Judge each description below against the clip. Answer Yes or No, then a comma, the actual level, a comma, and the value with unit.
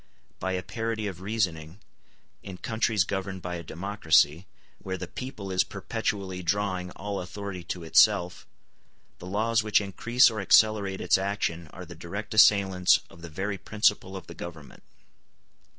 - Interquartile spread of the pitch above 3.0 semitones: No, average, 2.7 semitones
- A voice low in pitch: Yes, very low, 95 Hz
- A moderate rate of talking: Yes, average, 150 wpm